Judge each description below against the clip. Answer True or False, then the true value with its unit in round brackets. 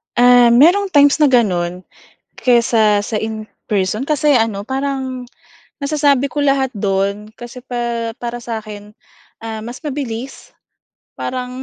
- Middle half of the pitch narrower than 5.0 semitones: True (3.8 semitones)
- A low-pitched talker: False (240 Hz)